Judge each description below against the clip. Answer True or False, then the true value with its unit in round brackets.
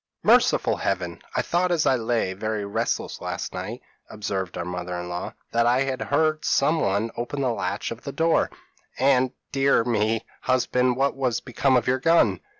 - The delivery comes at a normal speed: True (170 wpm)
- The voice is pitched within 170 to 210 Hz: False (120 Hz)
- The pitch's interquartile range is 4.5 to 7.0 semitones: True (5.0 semitones)